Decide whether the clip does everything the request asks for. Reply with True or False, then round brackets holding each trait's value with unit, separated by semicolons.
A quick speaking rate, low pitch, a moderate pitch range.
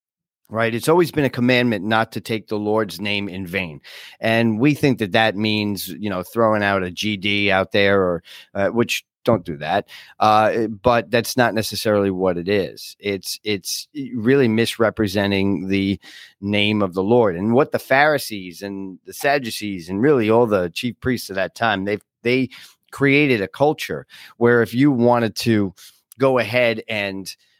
False (175 wpm; 110 Hz; 3.1 semitones)